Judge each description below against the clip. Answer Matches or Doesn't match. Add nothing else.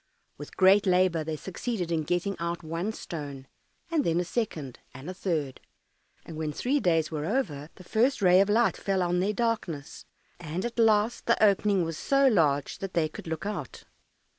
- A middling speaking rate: Matches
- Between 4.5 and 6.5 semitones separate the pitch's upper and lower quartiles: Matches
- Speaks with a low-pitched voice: Doesn't match